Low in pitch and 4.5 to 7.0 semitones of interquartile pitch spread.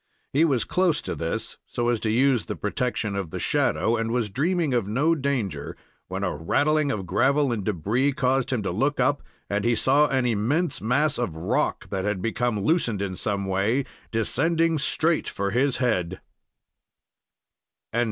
Yes: low, 120 Hz; wide, 5.6 semitones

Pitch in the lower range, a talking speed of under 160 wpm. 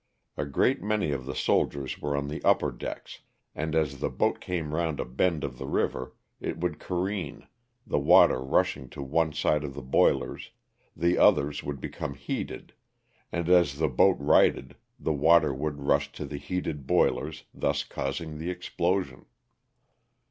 No: very low, 75 Hz; average, 165 wpm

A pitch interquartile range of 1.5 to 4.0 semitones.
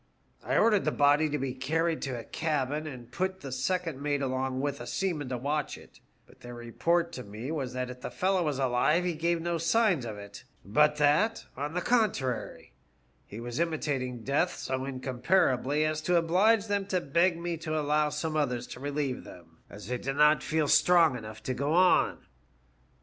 No: average, 4.6 semitones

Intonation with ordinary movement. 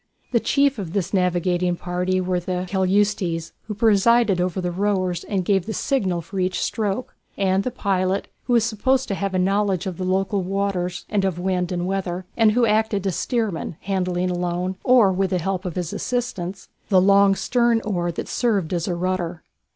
No: narrow, 2.3 semitones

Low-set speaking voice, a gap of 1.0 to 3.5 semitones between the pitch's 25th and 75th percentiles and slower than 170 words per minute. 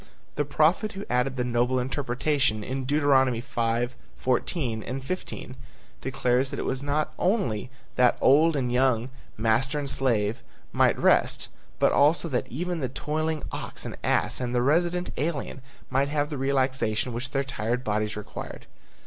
Yes: low, 130 Hz; average, 3.1 semitones; average, 150 wpm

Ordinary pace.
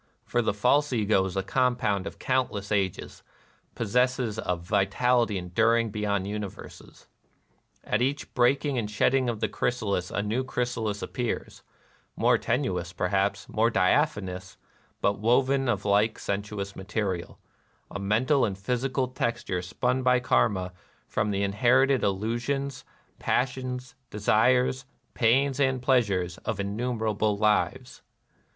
No: slow, 130 wpm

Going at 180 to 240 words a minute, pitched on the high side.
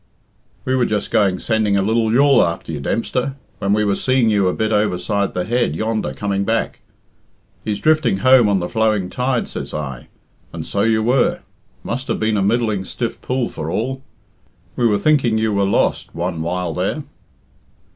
No: average, 185 wpm; low, 110 Hz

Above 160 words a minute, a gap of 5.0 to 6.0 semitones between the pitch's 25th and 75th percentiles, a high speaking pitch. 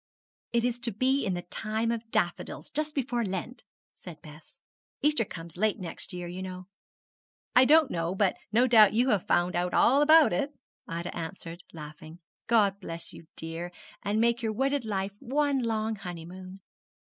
Yes: average, 170 wpm; wide, 5.5 semitones; high, 205 Hz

